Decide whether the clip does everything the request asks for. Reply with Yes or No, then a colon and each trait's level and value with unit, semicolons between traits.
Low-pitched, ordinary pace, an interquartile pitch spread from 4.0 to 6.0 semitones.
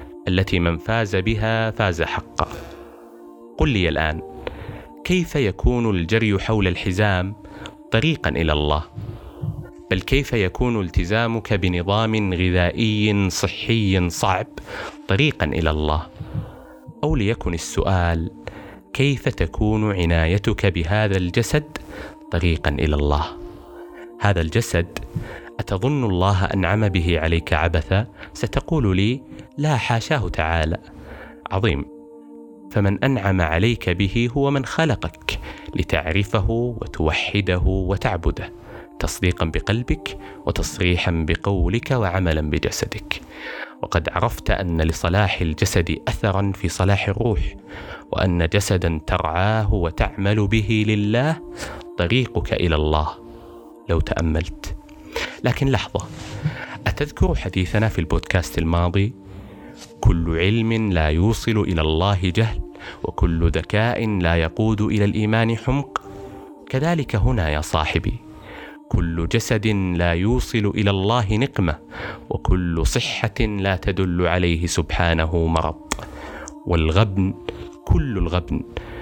Yes: low, 100 Hz; average, 100 wpm; average, 4.6 semitones